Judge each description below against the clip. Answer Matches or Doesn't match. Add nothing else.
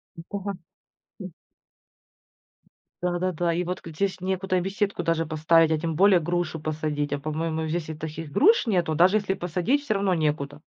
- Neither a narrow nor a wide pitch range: Matches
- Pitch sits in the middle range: Matches